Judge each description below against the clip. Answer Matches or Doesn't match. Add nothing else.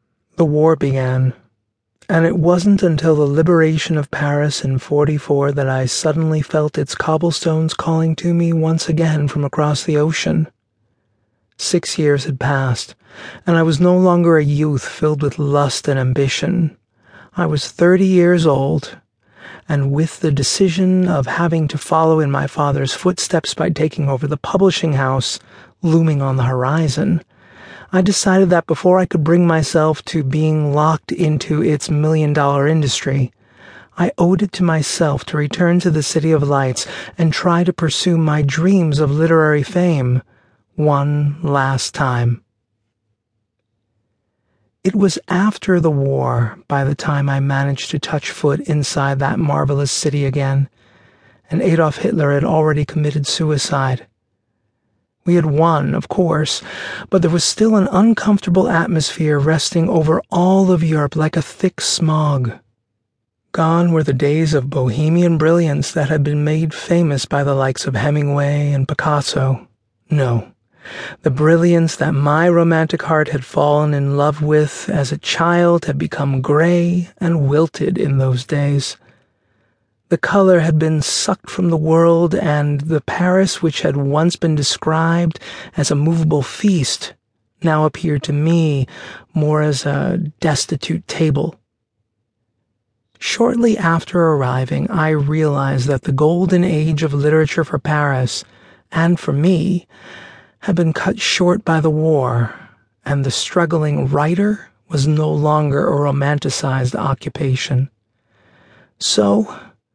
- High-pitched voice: Doesn't match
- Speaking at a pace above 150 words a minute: Doesn't match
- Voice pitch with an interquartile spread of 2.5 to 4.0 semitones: Matches